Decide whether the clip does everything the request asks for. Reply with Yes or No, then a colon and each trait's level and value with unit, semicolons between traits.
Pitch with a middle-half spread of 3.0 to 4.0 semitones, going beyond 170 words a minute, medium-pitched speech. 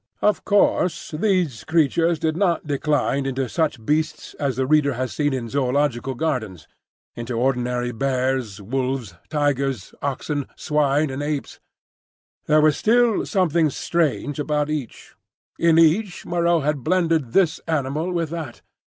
No: average, 3.7 semitones; slow, 135 wpm; medium, 145 Hz